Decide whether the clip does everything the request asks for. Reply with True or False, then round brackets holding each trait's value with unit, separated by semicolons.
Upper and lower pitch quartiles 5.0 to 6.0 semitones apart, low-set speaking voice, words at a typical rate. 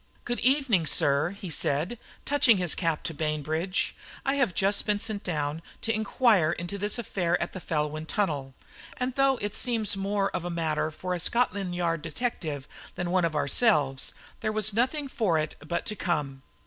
False (5.6 semitones; 180 Hz; 180 wpm)